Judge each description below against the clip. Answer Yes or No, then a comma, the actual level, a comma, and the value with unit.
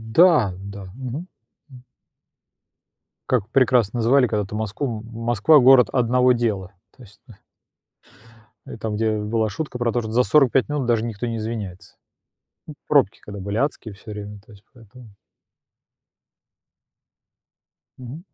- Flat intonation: No, average, 3.2 semitones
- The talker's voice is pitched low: Yes, low, 115 Hz